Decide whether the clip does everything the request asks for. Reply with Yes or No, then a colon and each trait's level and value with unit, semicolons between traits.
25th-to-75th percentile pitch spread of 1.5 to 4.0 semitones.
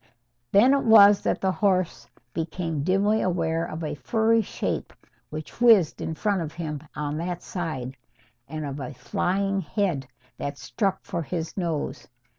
No: average, 4.4 semitones